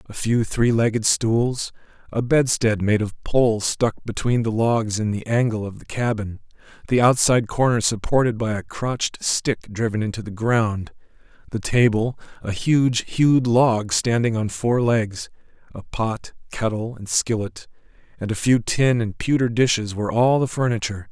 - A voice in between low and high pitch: No, low, 115 Hz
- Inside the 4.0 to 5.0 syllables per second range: Yes, 4.6 syllables/s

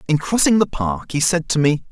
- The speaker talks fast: Yes, fast, 250 wpm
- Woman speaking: No, male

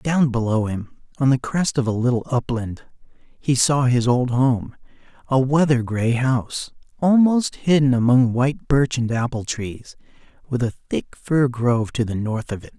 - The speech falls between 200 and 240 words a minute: No, average, 175 wpm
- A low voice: Yes, low, 125 Hz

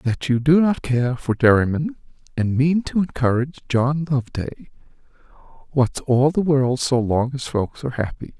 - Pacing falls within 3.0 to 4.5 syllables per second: No, 4.9 syllables/s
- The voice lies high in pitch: No, low, 135 Hz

